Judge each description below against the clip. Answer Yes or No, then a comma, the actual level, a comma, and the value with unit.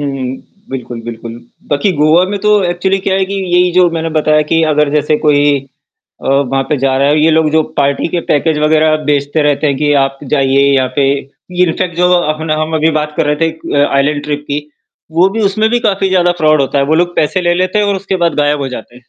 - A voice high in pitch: No, medium, 155 Hz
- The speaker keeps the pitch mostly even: No, average, 3.7 semitones